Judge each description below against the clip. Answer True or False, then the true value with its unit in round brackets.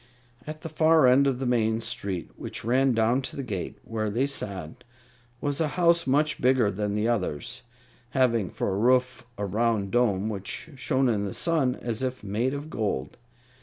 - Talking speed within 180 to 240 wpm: True (185 wpm)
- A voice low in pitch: True (120 Hz)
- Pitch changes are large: False (4.4 semitones)